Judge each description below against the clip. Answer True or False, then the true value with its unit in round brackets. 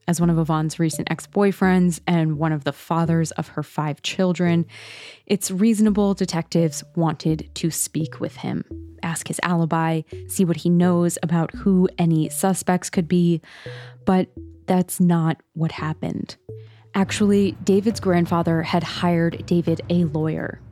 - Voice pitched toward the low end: False (170 Hz)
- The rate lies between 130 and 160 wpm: True (145 wpm)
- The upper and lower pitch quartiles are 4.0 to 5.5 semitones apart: False (2.6 semitones)